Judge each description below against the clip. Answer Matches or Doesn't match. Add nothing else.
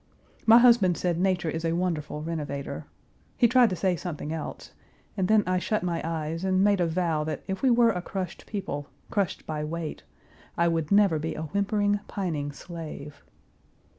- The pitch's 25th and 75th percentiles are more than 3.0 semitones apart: Matches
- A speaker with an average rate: Matches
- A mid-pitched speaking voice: Matches